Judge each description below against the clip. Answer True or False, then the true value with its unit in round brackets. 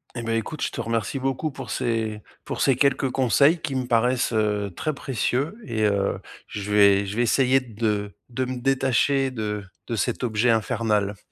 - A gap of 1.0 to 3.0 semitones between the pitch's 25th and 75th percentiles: False (3.8 semitones)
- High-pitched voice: False (115 Hz)